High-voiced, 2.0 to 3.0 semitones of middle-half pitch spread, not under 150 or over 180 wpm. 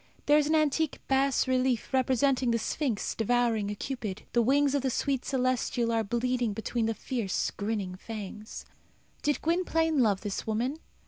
No: very high, 250 Hz; average, 3.6 semitones; average, 165 wpm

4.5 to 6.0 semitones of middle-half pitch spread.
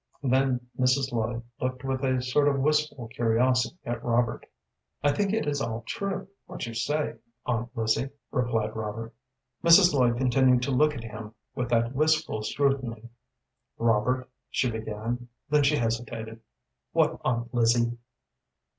No: average, 3.0 semitones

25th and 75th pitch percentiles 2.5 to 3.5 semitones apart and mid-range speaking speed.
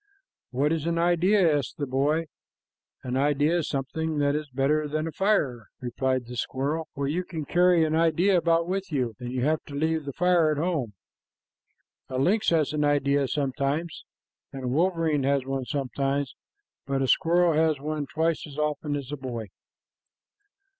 Yes: average, 3.2 semitones; average, 175 wpm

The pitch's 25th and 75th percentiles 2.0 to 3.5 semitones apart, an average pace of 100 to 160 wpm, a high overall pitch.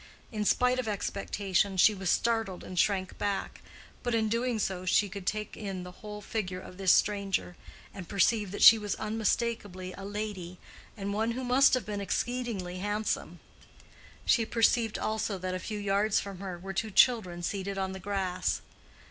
No: narrow, 2.6 semitones; average, 175 wpm; high, 205 Hz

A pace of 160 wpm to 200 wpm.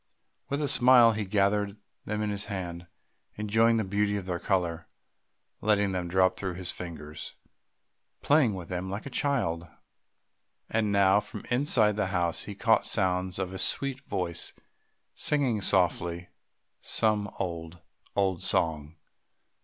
No: average, 140 wpm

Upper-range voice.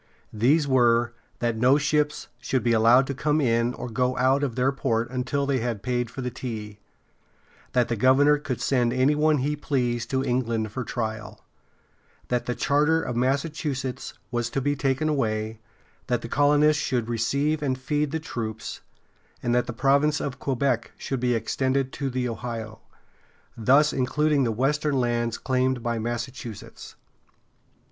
No: low, 130 Hz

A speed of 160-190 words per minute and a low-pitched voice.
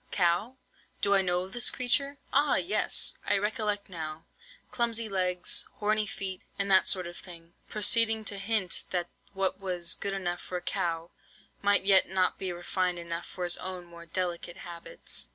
No: average, 170 wpm; medium, 185 Hz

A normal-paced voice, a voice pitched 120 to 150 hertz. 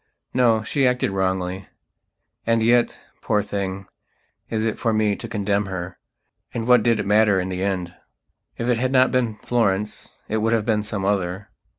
No: average, 175 wpm; low, 105 Hz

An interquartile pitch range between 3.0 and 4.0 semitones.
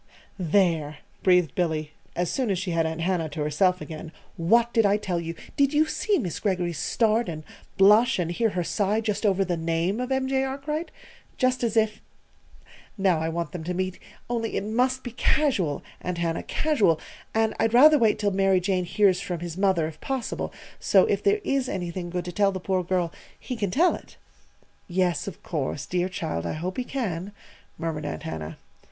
No: average, 4.9 semitones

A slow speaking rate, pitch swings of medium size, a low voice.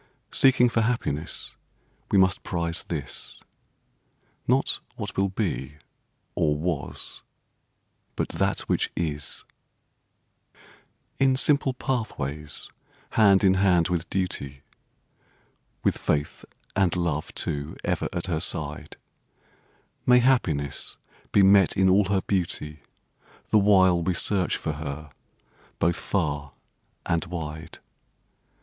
Yes: slow, 110 wpm; average, 4.5 semitones; very low, 90 Hz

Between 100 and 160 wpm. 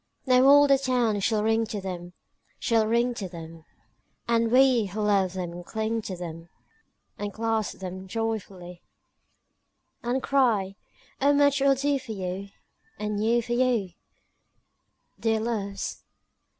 Yes: slow, 135 wpm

